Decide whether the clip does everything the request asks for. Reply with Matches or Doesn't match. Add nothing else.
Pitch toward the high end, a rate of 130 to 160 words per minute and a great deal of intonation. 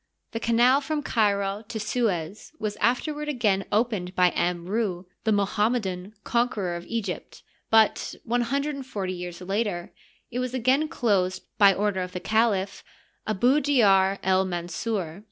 Doesn't match